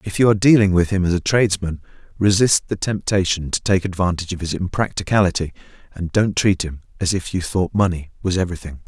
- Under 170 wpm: No, average, 195 wpm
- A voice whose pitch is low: Yes, very low, 95 Hz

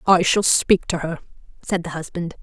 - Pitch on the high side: No, medium, 170 Hz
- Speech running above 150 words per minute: Yes, average, 200 wpm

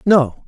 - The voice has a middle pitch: Yes, medium, 155 Hz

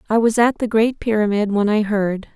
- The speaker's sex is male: No, female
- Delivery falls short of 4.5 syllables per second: No, 5.2 syllables/s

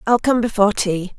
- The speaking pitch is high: Yes, high, 215 Hz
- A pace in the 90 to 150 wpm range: No, fast, 205 wpm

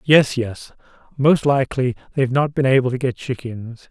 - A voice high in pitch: No, low, 130 Hz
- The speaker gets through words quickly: No, average, 170 wpm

